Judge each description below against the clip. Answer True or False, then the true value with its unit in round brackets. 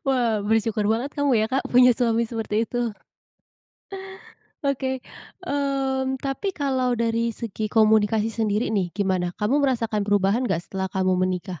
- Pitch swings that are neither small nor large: True (4.0 semitones)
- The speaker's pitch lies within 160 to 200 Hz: False (225 Hz)